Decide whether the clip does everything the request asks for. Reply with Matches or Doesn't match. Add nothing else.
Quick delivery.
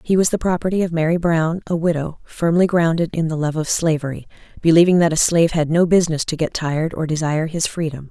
Matches